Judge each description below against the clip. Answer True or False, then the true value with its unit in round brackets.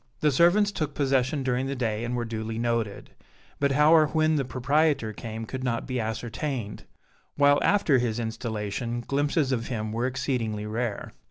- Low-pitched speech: True (125 Hz)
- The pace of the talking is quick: False (170 wpm)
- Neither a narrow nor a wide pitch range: True (4.0 semitones)